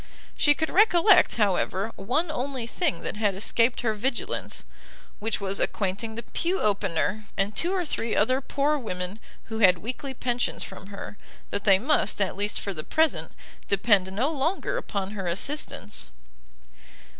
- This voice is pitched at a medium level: No, high, 220 Hz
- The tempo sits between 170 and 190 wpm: No, average, 155 wpm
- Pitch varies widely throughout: Yes, wide, 6.1 semitones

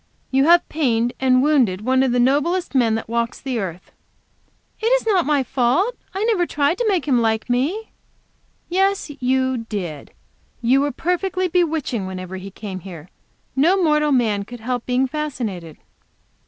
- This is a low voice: No, very high, 260 Hz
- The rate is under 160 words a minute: No, average, 165 wpm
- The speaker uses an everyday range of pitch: No, wide, 6.2 semitones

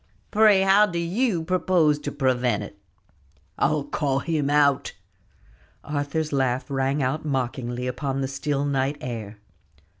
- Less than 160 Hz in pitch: Yes, medium, 140 Hz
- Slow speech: Yes, slow, 130 wpm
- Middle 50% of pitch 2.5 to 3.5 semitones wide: Yes, average, 3.2 semitones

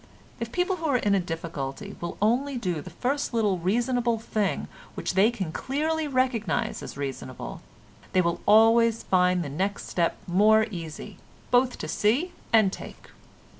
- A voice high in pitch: Yes, high, 215 Hz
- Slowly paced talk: No, average, 160 wpm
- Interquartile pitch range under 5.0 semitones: No, wide, 5.4 semitones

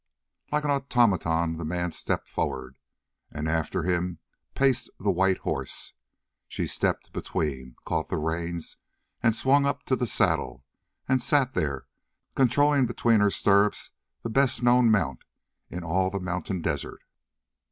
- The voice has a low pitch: Yes, very low, 95 Hz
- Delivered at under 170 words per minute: Yes, average, 140 wpm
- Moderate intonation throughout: No, wide, 7.3 semitones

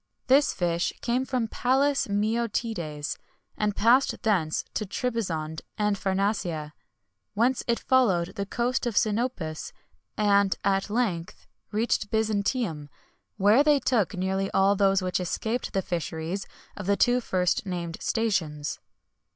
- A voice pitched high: Yes, high, 205 Hz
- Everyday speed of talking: No, slow, 125 wpm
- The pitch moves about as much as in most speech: Yes, average, 4.6 semitones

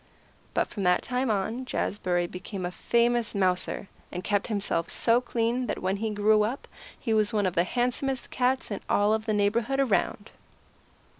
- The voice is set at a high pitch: Yes, high, 215 Hz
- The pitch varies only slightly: No, average, 3.6 semitones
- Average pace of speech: Yes, average, 180 wpm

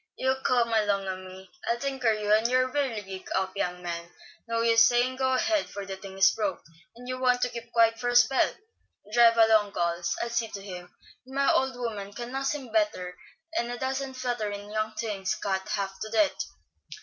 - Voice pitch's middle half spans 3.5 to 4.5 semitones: Yes, average, 4.0 semitones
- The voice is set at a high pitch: Yes, high, 225 Hz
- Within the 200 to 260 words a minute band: Yes, fast, 205 wpm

